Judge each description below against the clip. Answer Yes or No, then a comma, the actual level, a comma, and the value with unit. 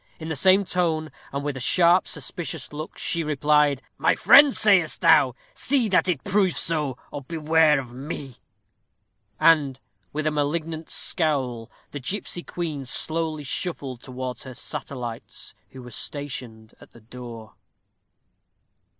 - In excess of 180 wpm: No, average, 140 wpm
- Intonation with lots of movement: No, average, 4.2 semitones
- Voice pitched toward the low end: No, medium, 150 Hz